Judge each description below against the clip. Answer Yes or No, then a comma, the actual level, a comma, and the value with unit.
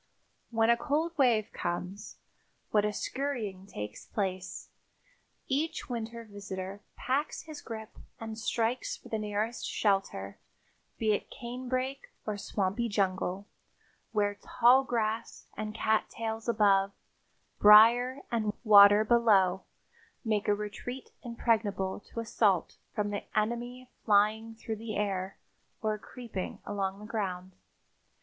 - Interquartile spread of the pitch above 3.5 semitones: No, average, 2.7 semitones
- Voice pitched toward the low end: No, high, 215 Hz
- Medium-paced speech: No, slow, 120 wpm